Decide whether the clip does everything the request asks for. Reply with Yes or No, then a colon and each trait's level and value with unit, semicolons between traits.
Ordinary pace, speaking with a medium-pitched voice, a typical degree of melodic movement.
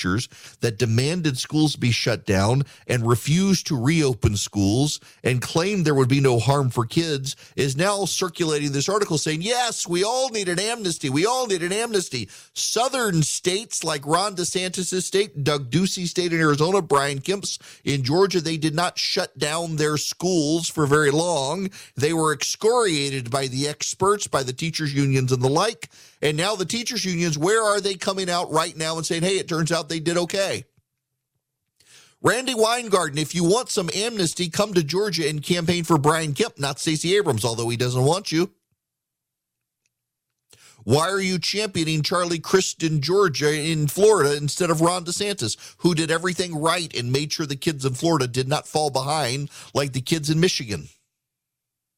Yes: average, 175 wpm; medium, 160 Hz; average, 4.7 semitones